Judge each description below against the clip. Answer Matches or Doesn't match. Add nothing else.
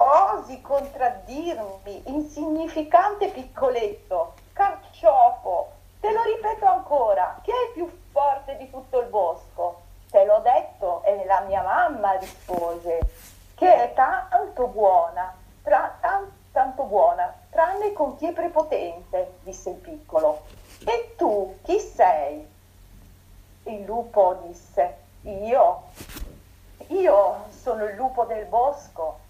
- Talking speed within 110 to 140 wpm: Matches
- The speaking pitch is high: Matches